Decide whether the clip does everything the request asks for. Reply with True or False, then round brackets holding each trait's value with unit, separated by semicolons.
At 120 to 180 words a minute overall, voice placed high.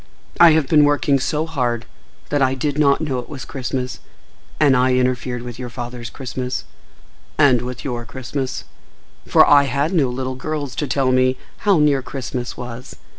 False (170 wpm; 130 Hz)